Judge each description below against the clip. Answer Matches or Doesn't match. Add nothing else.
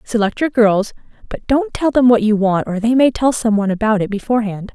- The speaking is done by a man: Doesn't match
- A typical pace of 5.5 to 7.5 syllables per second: Matches